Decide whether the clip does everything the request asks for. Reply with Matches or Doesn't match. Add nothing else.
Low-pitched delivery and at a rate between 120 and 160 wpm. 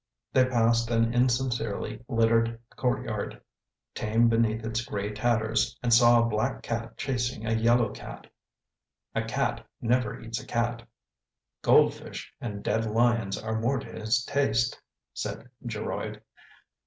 Matches